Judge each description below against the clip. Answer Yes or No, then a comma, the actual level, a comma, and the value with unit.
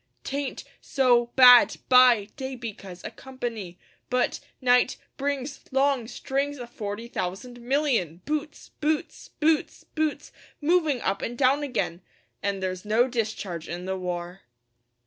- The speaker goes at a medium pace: No, slow, 130 wpm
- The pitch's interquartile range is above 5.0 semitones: Yes, wide, 5.6 semitones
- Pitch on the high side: Yes, high, 245 Hz